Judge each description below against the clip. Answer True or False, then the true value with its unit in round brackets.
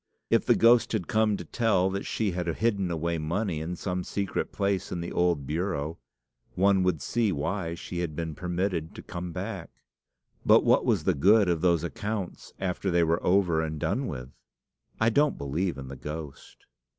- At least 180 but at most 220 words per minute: True (185 wpm)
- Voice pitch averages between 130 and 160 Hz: False (90 Hz)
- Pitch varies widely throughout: False (3.4 semitones)